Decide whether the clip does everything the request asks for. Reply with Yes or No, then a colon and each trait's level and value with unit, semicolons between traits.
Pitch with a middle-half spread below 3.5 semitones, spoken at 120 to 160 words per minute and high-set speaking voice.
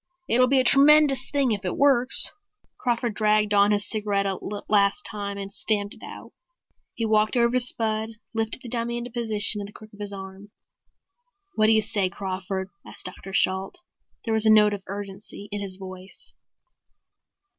No: average, 2.7 semitones; average, 180 wpm; high, 210 Hz